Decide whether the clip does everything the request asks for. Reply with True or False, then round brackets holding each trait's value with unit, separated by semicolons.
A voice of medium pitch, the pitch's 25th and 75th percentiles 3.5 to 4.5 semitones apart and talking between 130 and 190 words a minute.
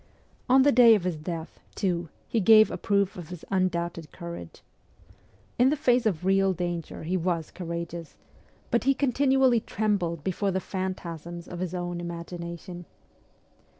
True (180 Hz; 3.9 semitones; 150 wpm)